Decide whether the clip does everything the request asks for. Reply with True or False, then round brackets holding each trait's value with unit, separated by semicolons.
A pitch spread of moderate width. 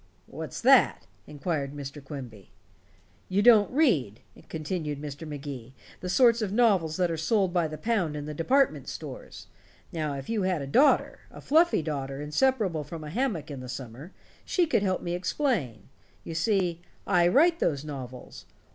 False (6.3 semitones)